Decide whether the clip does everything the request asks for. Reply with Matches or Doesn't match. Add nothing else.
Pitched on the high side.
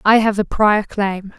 Matches